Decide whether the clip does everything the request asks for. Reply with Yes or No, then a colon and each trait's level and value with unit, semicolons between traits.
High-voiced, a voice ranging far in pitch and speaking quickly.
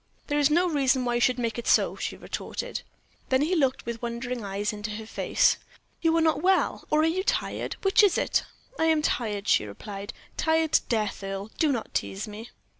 Yes: very high, 250 Hz; wide, 6.9 semitones; fast, 210 wpm